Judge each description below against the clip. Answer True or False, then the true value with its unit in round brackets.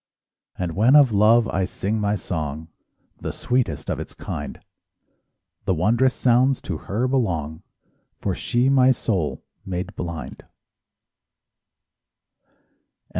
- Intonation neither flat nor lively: False (6.2 semitones)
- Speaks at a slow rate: True (115 wpm)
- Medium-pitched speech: False (105 Hz)